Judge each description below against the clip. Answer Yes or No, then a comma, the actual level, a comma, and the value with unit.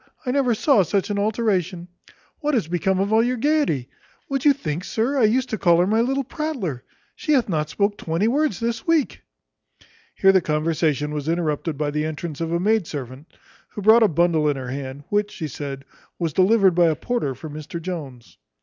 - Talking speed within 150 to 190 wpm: No, fast, 205 wpm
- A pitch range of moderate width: No, wide, 6.8 semitones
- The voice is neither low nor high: Yes, medium, 180 Hz